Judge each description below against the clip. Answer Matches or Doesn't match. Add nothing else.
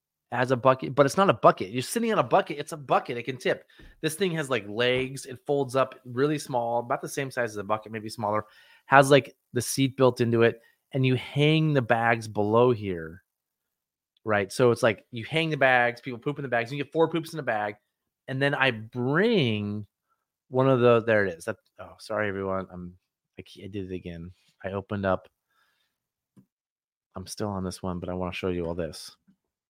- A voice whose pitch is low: Matches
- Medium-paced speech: Doesn't match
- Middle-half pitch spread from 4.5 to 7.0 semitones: Matches